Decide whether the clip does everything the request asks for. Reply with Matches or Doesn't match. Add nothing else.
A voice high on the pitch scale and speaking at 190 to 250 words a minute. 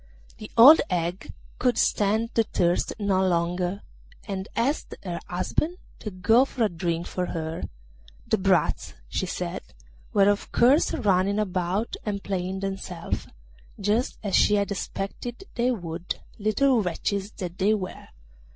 Doesn't match